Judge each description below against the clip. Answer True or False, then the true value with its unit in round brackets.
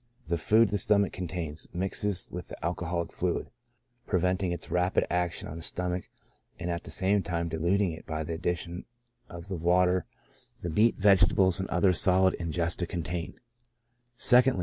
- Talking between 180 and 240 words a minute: False (165 wpm)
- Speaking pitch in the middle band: False (90 Hz)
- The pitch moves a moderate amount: False (1.8 semitones)